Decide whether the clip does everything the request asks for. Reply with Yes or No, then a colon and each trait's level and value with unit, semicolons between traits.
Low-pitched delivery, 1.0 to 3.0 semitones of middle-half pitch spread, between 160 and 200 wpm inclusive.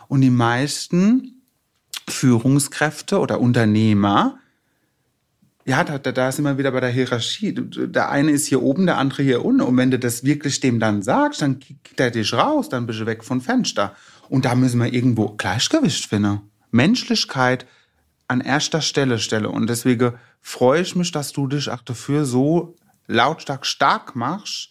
No: low, 130 Hz; average, 3.4 semitones; average, 170 wpm